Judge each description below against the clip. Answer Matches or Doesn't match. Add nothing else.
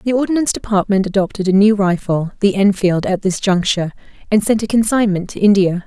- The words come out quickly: Doesn't match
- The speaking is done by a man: Doesn't match